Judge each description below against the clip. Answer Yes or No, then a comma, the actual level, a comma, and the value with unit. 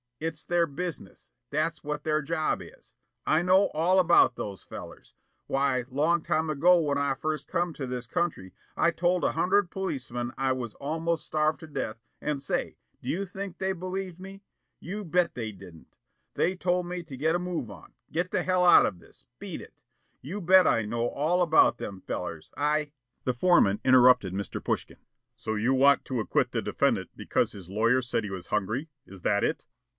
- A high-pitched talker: No, medium, 155 Hz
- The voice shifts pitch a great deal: Yes, wide, 5.9 semitones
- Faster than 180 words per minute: Yes, average, 190 wpm